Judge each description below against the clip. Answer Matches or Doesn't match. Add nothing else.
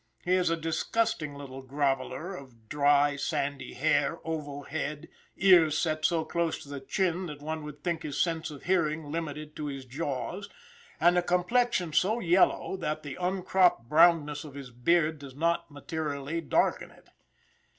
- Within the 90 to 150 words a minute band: Doesn't match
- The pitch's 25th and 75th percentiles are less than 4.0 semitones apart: Matches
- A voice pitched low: Doesn't match